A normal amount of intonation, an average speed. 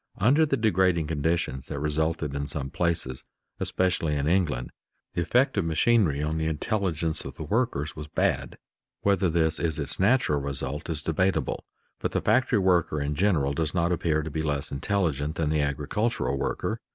Yes: average, 4.2 semitones; average, 175 wpm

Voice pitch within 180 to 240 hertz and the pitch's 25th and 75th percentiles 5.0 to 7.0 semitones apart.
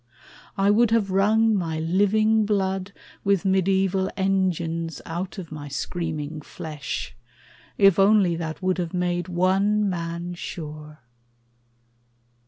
No: medium, 185 Hz; average, 2.9 semitones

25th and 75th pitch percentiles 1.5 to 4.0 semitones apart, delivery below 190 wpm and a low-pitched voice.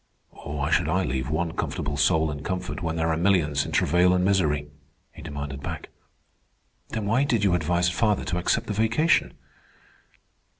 No: average, 4.7 semitones; average, 170 wpm; very low, 85 Hz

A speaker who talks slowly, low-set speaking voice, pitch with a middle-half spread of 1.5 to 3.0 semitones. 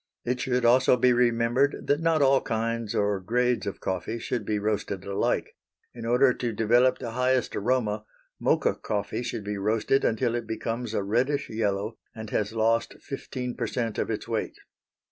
No: average, 175 wpm; low, 115 Hz; average, 2.7 semitones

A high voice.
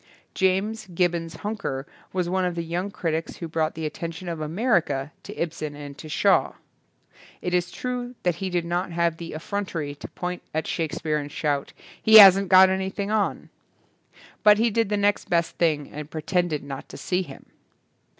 No: medium, 175 Hz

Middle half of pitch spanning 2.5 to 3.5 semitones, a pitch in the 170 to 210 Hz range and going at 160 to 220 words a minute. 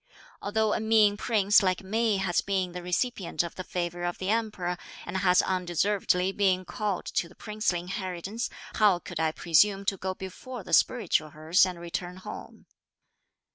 Yes: average, 2.9 semitones; medium, 185 Hz; average, 170 wpm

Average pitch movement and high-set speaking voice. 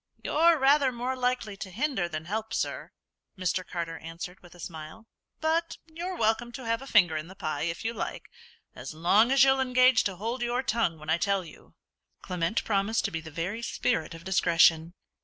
No: wide, 6.9 semitones; high, 200 Hz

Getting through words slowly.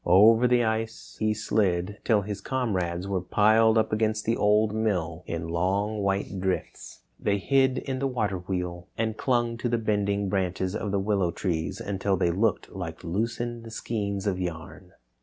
No: average, 170 wpm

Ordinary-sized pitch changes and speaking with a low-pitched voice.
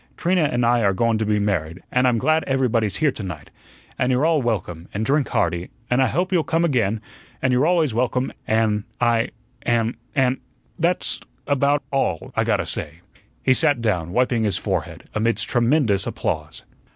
Yes: average, 4.5 semitones; low, 120 Hz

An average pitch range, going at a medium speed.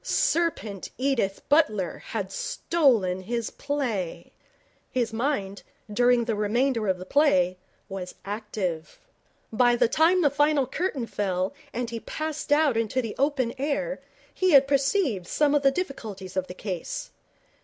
No: wide, 6.3 semitones; average, 145 wpm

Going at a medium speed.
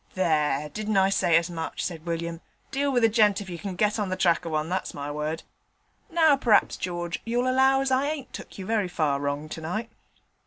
No: fast, 220 wpm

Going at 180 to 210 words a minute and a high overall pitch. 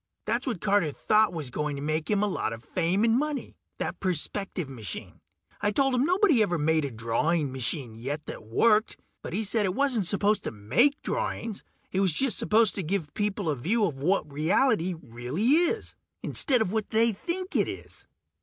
Yes: average, 195 wpm; high, 195 Hz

